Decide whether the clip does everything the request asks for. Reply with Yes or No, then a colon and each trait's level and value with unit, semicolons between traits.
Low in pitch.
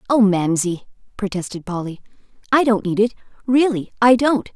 No: high, 215 Hz